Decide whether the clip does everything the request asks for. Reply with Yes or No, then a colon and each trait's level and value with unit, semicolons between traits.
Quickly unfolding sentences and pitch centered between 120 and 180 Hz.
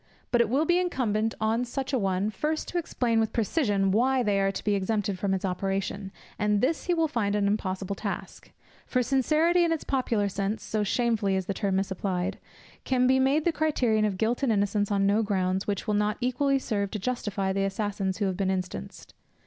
No: fast, 210 wpm; high, 210 Hz